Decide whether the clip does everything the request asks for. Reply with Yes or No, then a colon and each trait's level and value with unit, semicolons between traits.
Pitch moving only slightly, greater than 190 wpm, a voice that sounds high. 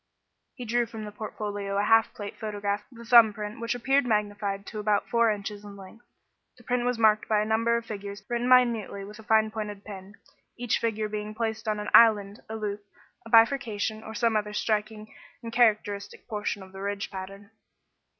Yes: narrow, 1.9 semitones; average, 200 wpm; high, 215 Hz